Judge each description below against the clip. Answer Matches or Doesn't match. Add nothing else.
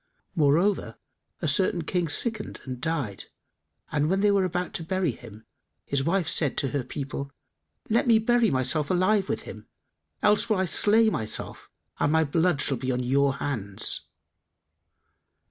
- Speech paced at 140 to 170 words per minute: Matches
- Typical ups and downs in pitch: Doesn't match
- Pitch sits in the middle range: Matches